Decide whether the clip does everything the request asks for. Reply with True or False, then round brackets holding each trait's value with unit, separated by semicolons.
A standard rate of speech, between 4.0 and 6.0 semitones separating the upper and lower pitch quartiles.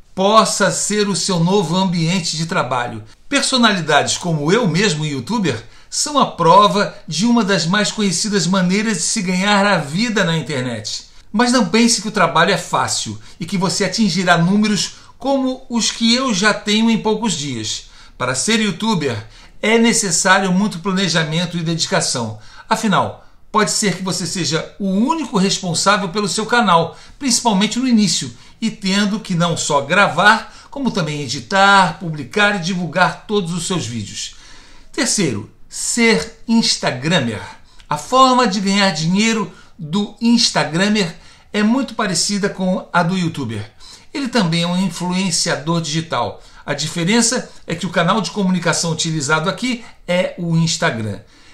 True (150 wpm; 4.5 semitones)